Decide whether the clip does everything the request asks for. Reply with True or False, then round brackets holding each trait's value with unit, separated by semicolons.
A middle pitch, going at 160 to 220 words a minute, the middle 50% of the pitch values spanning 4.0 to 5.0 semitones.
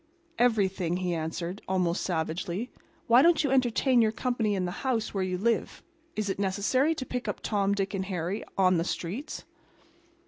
False (200 Hz; 175 wpm; 4.7 semitones)